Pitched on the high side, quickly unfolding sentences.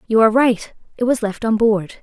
Yes: high, 225 Hz; fast, 235 wpm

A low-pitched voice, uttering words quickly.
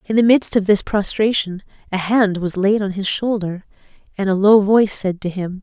No: high, 200 Hz; fast, 215 wpm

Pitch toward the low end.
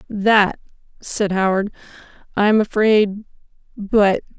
No: high, 205 Hz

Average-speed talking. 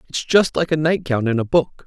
No: fast, 290 wpm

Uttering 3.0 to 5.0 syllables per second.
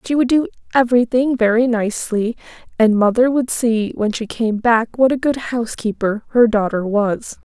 Yes: 4.9 syllables/s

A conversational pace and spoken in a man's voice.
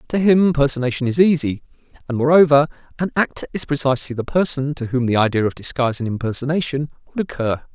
Yes: average, 180 wpm; male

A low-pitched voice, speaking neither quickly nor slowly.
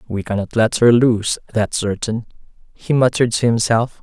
Yes: low, 115 Hz; average, 165 wpm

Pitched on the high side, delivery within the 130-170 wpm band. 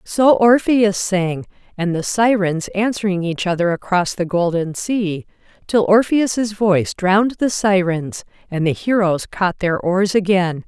Yes: high, 195 Hz; average, 145 wpm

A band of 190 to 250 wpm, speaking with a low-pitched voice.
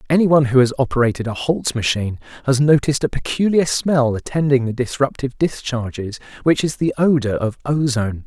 No: average, 160 wpm; low, 130 Hz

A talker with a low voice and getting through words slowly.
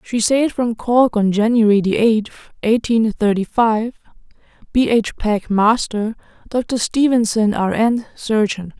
No: high, 220 Hz; slow, 130 wpm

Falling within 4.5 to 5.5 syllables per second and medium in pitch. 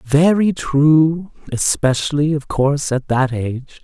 No: 4.0 syllables/s; medium, 145 Hz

